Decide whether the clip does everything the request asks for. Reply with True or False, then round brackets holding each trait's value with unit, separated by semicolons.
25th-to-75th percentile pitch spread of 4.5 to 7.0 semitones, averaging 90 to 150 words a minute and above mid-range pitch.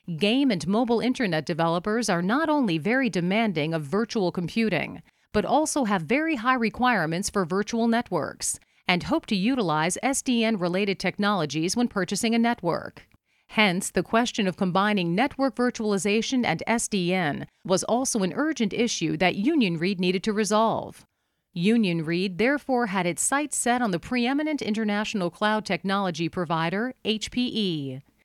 True (4.9 semitones; 140 wpm; 210 Hz)